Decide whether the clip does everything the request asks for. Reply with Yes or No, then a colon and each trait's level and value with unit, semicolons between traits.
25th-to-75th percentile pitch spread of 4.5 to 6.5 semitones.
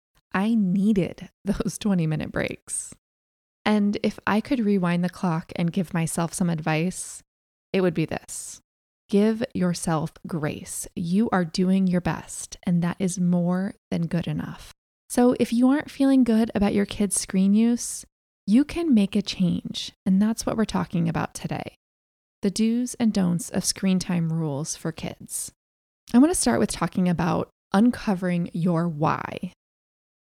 No: average, 4.0 semitones